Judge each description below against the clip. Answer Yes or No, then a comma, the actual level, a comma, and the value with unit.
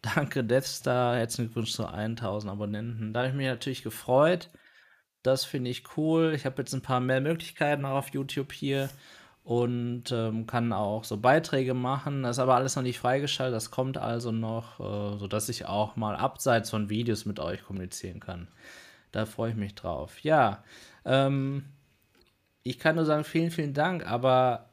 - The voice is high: No, low, 125 Hz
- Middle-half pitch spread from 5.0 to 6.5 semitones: No, average, 3.7 semitones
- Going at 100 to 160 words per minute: No, average, 175 wpm